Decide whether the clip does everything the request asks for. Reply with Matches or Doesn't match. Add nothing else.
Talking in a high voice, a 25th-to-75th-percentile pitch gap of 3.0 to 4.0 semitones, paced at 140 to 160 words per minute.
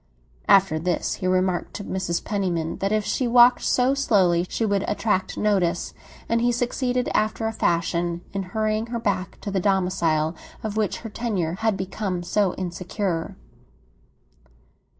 Matches